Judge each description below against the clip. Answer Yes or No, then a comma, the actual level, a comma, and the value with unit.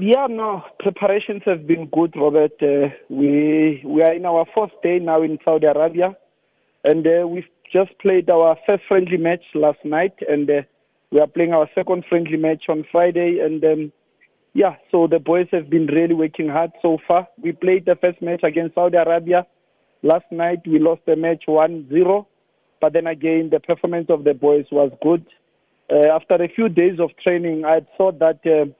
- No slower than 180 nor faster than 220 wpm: Yes, average, 190 wpm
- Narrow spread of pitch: Yes, narrow, 2.3 semitones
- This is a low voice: No, medium, 165 Hz